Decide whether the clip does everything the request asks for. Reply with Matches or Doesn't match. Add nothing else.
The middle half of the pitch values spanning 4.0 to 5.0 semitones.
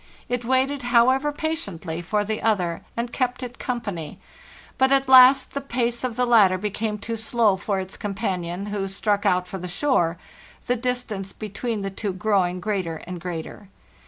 Matches